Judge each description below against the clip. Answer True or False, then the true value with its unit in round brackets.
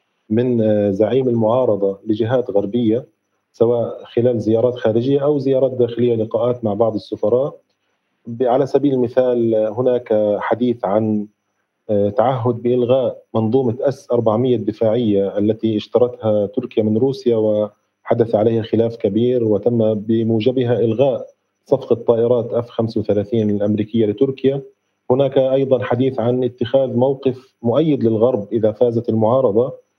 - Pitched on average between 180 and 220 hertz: False (115 Hz)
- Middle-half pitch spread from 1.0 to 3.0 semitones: True (2.6 semitones)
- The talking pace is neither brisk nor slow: True (115 wpm)